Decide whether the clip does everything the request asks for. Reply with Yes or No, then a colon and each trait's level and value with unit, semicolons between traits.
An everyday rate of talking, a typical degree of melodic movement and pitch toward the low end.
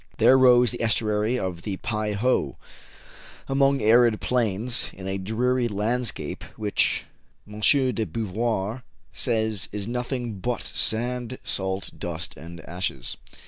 No: slow, 125 wpm; average, 3.9 semitones; low, 110 Hz